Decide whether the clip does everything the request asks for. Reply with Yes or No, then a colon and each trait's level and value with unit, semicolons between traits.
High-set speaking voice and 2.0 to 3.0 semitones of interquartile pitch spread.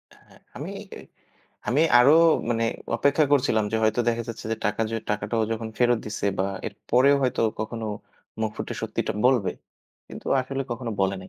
No: low, 115 Hz; narrow, 2.6 semitones